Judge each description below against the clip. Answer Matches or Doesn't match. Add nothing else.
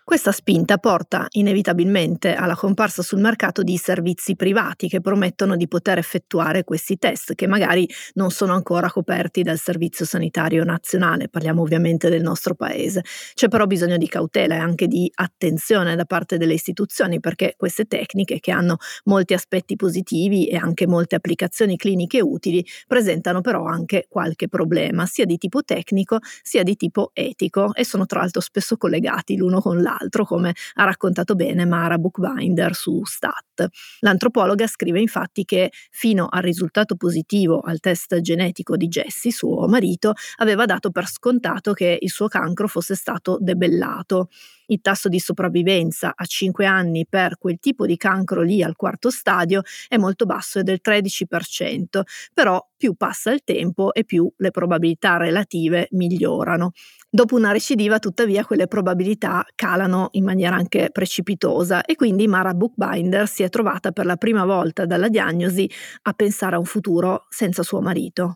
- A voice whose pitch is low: Doesn't match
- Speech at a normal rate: Matches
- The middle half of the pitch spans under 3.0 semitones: Matches